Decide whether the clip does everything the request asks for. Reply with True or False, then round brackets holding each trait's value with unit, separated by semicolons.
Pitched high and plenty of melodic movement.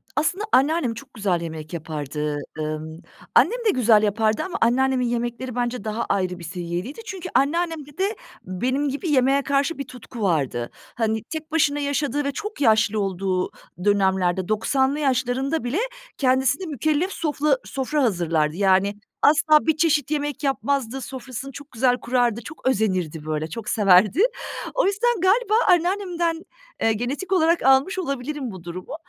True (255 Hz; 7.0 semitones)